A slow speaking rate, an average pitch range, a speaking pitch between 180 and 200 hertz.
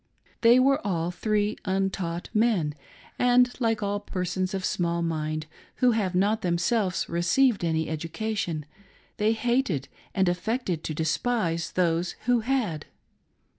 Yes: slow, 130 wpm; average, 5.0 semitones; high, 190 Hz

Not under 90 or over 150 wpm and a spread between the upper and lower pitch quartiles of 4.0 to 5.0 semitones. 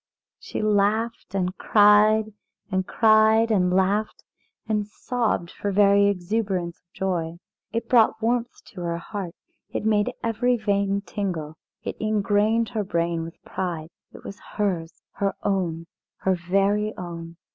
No: slow, 135 wpm; average, 3.2 semitones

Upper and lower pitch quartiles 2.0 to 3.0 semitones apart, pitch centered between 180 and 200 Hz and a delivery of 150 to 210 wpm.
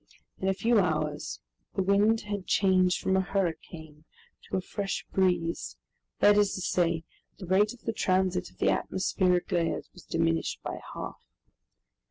Yes: narrow, 2.6 semitones; medium, 185 Hz; average, 160 wpm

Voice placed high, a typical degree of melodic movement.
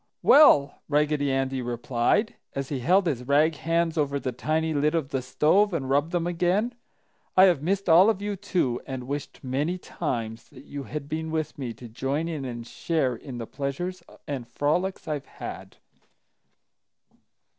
No: medium, 145 Hz; average, 4.2 semitones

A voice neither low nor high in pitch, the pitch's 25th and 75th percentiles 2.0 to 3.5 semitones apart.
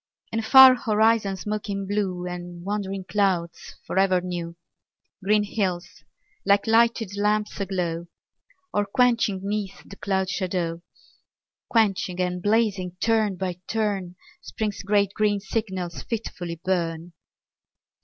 No: high, 195 Hz; average, 2.8 semitones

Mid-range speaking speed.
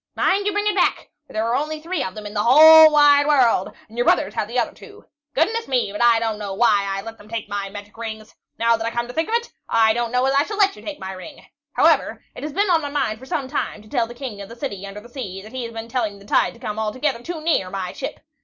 No: fast, 295 wpm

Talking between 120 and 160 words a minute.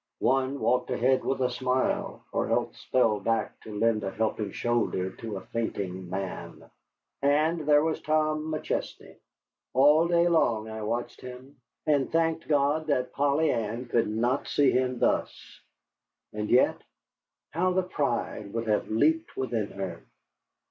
Yes: average, 150 wpm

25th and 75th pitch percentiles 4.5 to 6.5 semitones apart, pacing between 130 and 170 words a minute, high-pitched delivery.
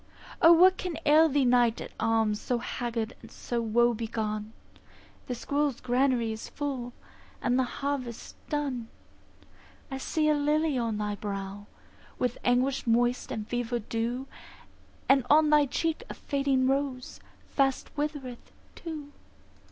No: average, 3.7 semitones; average, 140 wpm; very high, 250 Hz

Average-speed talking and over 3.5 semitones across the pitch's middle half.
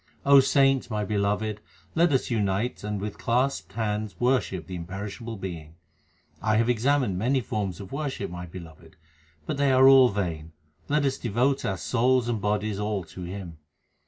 Yes: average, 160 wpm; average, 4.8 semitones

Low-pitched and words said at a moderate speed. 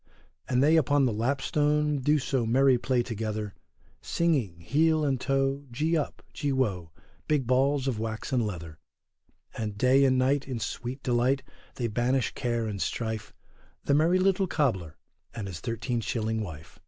Yes: low, 125 Hz; average, 160 wpm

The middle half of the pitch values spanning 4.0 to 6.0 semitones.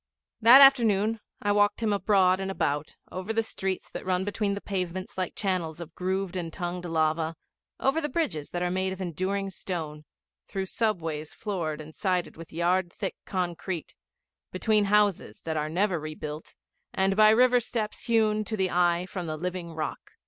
No: average, 3.4 semitones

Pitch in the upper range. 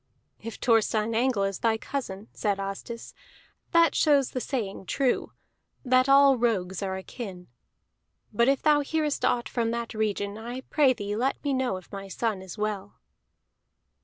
Yes: high, 230 Hz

